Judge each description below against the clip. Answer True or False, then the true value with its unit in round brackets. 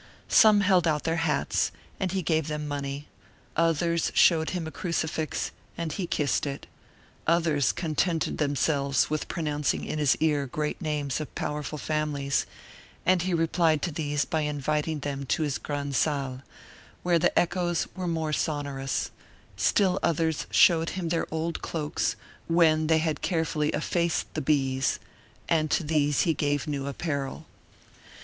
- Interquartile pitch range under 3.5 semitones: True (2.4 semitones)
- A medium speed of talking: True (150 wpm)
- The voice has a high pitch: False (155 Hz)